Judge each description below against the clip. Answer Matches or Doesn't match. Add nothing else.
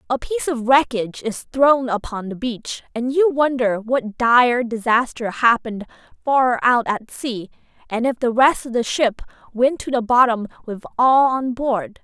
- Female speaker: Matches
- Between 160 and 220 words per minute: Matches